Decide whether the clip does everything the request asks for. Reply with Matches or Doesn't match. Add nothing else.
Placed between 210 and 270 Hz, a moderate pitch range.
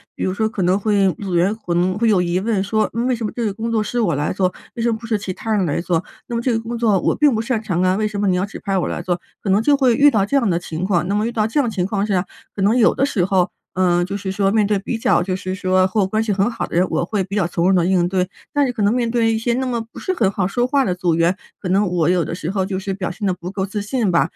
Doesn't match